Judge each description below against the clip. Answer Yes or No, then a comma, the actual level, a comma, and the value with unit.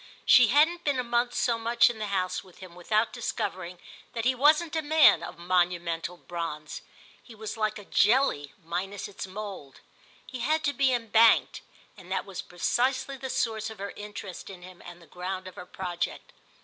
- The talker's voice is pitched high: Yes, high, 210 Hz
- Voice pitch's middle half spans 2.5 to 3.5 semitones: No, average, 5.3 semitones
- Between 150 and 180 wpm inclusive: No, average, 190 wpm